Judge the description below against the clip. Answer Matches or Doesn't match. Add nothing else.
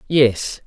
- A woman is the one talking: Matches